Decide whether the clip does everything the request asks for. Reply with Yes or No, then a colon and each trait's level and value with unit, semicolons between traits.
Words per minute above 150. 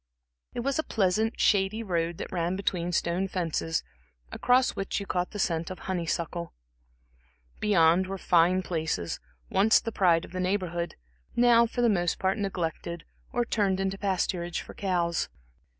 Yes: average, 160 wpm